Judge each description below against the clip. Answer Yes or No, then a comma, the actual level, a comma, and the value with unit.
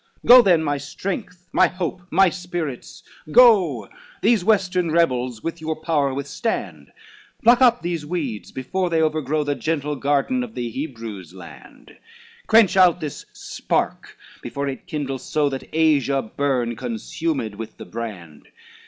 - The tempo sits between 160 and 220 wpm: No, average, 145 wpm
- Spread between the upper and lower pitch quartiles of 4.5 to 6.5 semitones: Yes, average, 5.3 semitones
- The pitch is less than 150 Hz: No, medium, 155 Hz